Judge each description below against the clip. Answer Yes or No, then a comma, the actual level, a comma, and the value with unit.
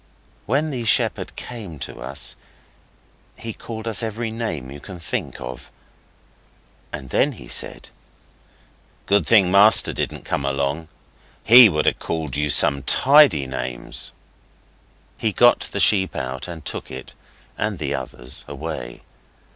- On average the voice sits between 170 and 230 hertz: No, very low, 85 Hz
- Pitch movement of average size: No, wide, 8.3 semitones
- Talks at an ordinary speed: No, slow, 130 wpm